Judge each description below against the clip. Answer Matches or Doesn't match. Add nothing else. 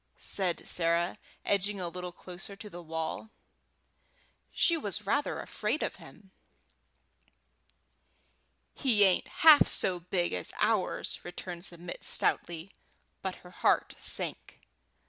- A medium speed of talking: Doesn't match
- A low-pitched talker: Doesn't match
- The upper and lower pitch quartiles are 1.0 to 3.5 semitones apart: Matches